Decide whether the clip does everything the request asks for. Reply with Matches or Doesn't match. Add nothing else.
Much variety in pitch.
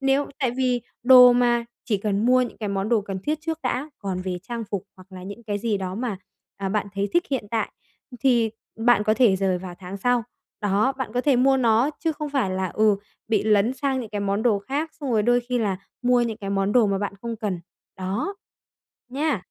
Doesn't match